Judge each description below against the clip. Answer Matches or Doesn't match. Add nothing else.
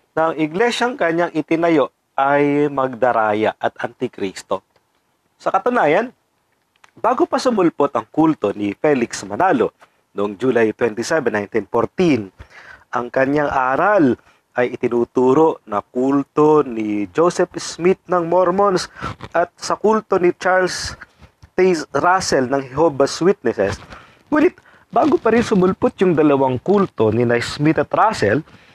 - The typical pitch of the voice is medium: Matches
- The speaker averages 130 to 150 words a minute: Doesn't match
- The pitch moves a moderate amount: Doesn't match